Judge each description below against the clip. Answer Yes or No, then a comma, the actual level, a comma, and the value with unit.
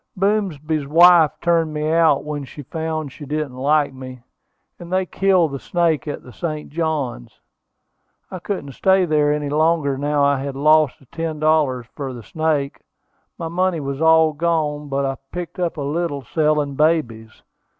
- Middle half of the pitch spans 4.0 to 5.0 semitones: No, average, 2.8 semitones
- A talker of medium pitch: Yes, medium, 150 Hz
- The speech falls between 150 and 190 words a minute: Yes, average, 170 wpm